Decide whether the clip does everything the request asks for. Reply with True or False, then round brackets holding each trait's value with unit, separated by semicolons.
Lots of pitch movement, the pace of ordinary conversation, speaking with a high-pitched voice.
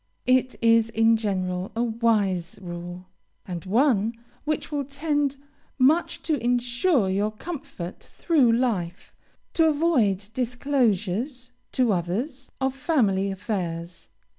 False (5.8 semitones; 115 wpm; 230 Hz)